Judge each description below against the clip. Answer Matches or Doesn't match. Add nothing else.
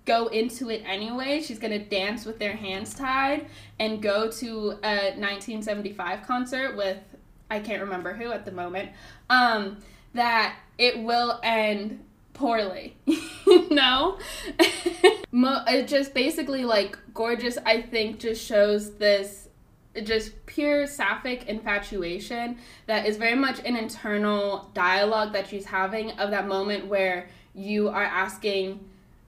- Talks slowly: Matches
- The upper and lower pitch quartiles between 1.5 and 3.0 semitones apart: Doesn't match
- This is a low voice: Doesn't match